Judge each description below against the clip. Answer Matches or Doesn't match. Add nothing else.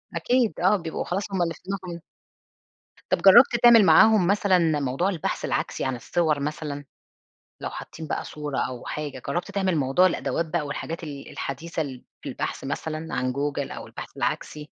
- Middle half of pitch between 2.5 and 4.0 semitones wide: Doesn't match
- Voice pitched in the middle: Matches